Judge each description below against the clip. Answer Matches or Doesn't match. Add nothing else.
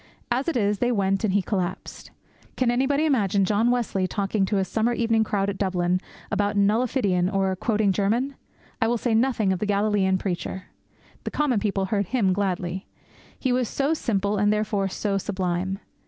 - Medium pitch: Doesn't match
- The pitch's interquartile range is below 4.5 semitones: Matches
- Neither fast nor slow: Matches